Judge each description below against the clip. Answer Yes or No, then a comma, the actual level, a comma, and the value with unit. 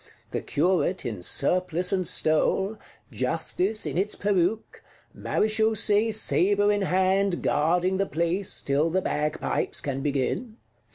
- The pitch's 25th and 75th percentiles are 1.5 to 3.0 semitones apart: No, average, 4.5 semitones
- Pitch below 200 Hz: Yes, medium, 185 Hz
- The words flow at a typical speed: No, slow, 120 wpm